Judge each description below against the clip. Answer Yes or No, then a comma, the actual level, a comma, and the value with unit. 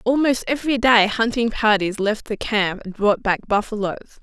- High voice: Yes, high, 220 Hz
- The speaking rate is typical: Yes, average, 170 wpm